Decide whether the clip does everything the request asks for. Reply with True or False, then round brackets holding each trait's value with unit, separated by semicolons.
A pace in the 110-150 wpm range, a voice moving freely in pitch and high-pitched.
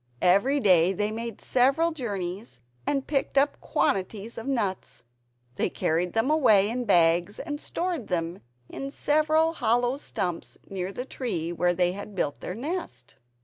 True (145 wpm; 7.1 semitones; 215 Hz)